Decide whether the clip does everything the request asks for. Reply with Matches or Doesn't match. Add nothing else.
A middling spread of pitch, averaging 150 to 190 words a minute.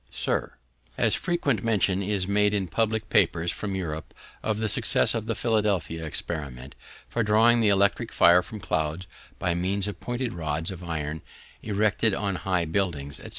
Matches